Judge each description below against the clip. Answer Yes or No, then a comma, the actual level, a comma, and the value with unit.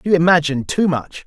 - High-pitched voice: No, medium, 160 Hz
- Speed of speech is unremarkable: Yes, average, 190 wpm